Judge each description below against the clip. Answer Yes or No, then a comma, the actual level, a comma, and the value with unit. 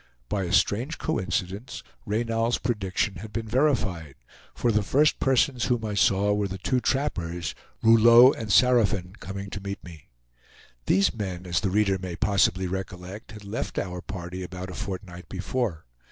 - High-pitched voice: No, low, 100 Hz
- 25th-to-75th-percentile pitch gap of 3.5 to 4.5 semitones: Yes, average, 3.8 semitones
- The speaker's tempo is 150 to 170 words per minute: Yes, average, 160 wpm